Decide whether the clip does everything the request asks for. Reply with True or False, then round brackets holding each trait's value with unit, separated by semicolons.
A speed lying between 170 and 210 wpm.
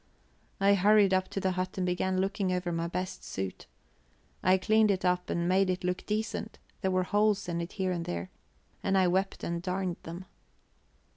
True (195 wpm)